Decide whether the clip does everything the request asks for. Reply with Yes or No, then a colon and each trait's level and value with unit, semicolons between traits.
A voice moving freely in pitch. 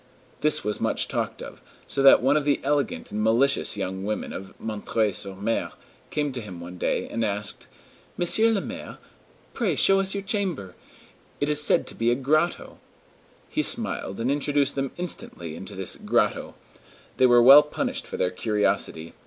Yes: wide, 6.4 semitones